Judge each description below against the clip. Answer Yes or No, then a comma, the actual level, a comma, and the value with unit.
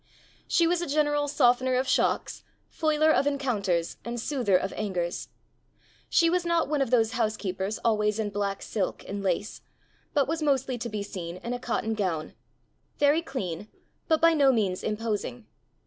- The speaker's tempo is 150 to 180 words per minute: Yes, average, 165 wpm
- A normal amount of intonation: No, wide, 6.3 semitones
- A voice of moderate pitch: No, high, 235 Hz